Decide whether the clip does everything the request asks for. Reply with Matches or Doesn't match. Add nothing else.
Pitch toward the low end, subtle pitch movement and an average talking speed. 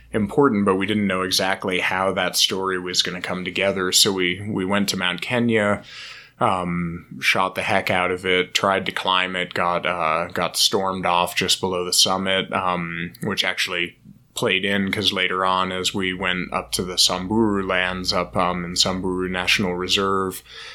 Matches